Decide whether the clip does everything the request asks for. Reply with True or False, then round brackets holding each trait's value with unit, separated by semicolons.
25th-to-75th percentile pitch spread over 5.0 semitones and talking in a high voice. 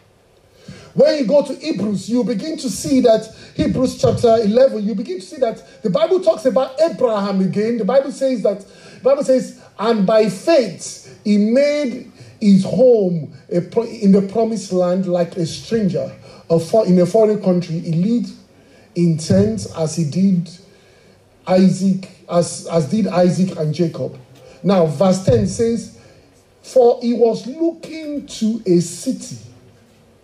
True (5.5 semitones; 205 Hz)